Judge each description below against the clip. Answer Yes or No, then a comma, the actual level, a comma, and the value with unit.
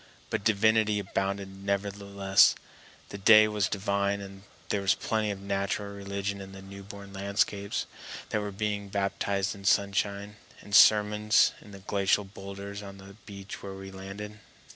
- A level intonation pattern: Yes, narrow, 0.8 semitones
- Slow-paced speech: No, average, 150 wpm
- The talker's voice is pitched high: No, low, 100 Hz